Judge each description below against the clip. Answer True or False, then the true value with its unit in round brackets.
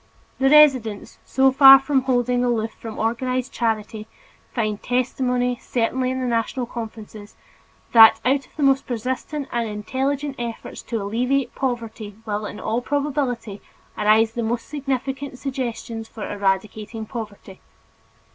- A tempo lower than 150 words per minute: True (135 wpm)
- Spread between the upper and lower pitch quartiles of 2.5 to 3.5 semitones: True (3.1 semitones)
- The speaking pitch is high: True (240 Hz)